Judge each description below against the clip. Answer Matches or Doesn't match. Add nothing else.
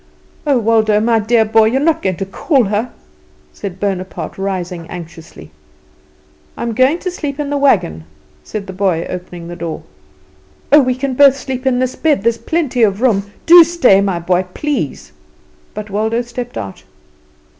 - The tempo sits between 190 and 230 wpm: Doesn't match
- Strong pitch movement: Matches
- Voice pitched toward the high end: Matches